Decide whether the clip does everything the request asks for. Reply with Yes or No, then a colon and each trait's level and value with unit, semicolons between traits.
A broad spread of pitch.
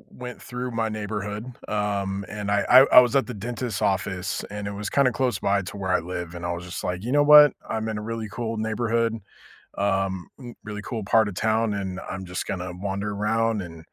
No: average, 2.8 semitones